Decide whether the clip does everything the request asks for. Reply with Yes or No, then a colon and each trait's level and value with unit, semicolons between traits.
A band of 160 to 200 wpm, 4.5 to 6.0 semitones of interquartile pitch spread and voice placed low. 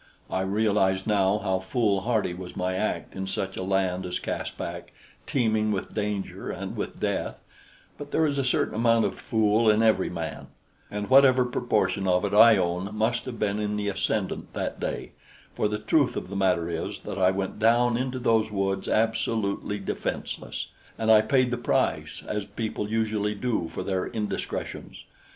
No: average, 175 wpm; average, 2.8 semitones; low, 105 Hz